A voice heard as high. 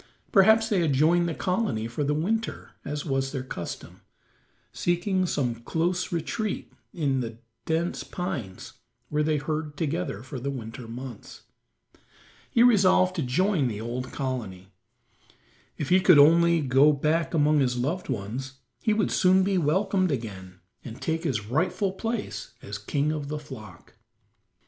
No: medium, 150 Hz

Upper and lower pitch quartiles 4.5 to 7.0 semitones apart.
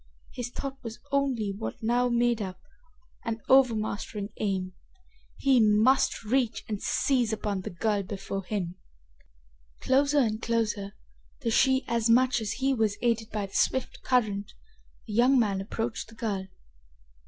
No: average, 3.4 semitones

